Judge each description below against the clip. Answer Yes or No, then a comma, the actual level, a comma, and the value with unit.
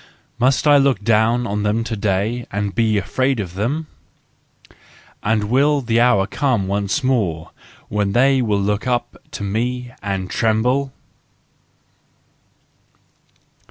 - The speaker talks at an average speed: No, slow, 125 wpm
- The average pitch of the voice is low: Yes, low, 115 Hz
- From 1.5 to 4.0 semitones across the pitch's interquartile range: Yes, average, 3.7 semitones